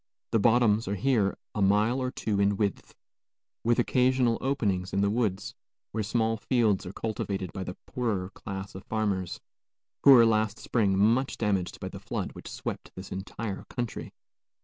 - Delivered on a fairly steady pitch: No, average, 3.2 semitones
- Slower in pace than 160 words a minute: No, average, 170 wpm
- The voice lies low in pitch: Yes, low, 105 Hz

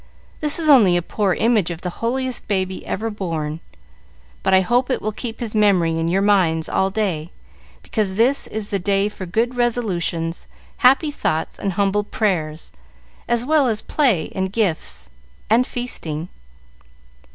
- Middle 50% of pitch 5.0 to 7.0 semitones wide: Yes, average, 5.3 semitones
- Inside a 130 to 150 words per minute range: No, average, 160 wpm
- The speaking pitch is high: Yes, high, 200 Hz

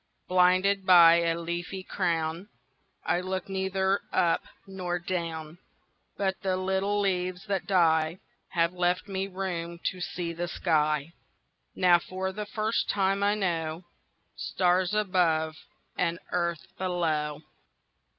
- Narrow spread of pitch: Yes, narrow, 2.2 semitones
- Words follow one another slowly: Yes, slow, 105 wpm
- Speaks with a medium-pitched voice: Yes, medium, 180 Hz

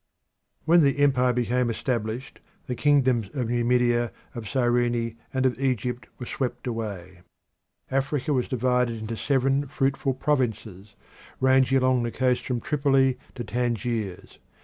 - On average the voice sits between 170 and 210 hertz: No, low, 125 Hz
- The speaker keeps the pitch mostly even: Yes, narrow, 2.2 semitones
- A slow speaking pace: Yes, slow, 130 wpm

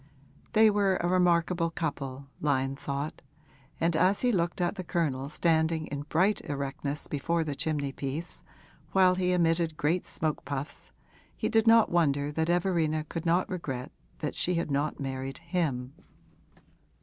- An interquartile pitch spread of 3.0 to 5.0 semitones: Yes, average, 3.8 semitones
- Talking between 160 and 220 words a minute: No, average, 150 wpm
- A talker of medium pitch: Yes, medium, 160 Hz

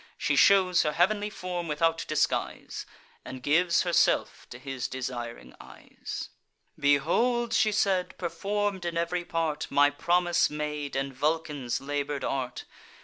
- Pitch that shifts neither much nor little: Yes, average, 4.1 semitones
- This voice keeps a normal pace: No, slow, 130 wpm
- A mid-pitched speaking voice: Yes, medium, 160 Hz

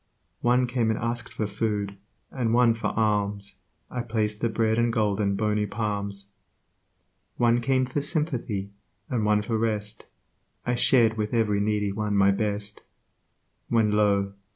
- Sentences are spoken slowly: No, average, 155 wpm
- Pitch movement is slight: Yes, narrow, 2.3 semitones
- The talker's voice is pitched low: Yes, low, 110 Hz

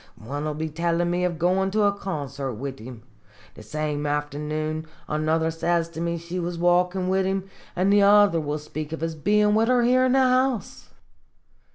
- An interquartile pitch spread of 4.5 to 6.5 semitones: No, average, 4.1 semitones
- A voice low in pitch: No, medium, 170 Hz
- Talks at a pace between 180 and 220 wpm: Yes, average, 195 wpm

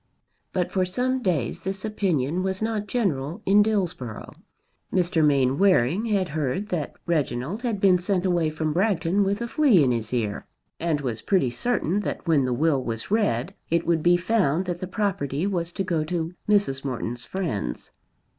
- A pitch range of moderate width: No, wide, 5.9 semitones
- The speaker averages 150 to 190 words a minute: Yes, average, 175 wpm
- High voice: No, medium, 175 Hz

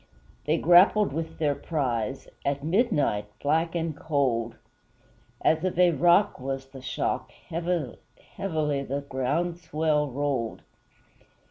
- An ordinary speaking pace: No, slow, 115 wpm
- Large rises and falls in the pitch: No, average, 3.7 semitones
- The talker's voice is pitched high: No, medium, 150 Hz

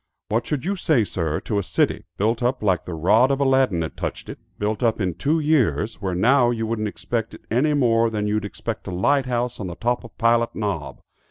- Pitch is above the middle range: No, low, 115 Hz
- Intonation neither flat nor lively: Yes, average, 3.9 semitones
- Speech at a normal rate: No, fast, 230 wpm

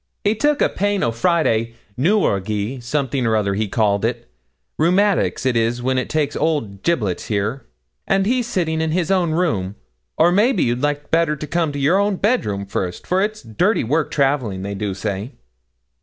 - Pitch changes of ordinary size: No, wide, 8.3 semitones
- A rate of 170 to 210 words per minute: Yes, average, 185 wpm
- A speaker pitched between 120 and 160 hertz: Yes, medium, 140 Hz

